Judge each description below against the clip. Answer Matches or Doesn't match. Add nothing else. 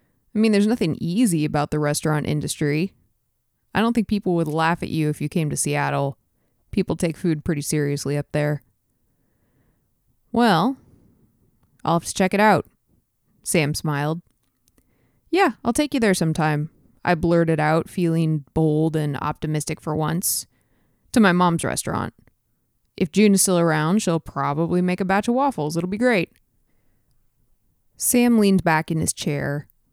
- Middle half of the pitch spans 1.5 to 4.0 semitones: Doesn't match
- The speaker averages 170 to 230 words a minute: Doesn't match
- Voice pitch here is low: Doesn't match